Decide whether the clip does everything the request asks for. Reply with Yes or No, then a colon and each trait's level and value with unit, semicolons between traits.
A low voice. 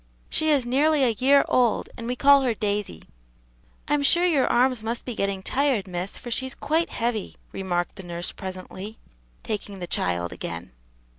No: high, 230 Hz